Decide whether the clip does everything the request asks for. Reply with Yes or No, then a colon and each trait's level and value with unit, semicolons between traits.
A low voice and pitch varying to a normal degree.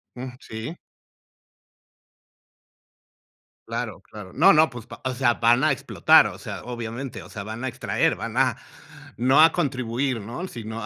Yes: low, 120 Hz; average, 3.4 semitones